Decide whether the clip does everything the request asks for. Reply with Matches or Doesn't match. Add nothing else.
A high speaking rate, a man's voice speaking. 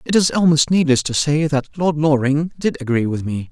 Matches